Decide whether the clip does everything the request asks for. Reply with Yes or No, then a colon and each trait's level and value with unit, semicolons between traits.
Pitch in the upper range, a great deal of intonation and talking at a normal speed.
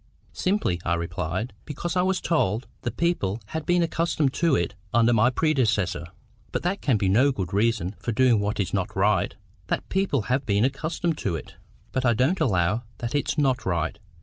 No: low, 120 Hz; wide, 7.6 semitones; average, 185 wpm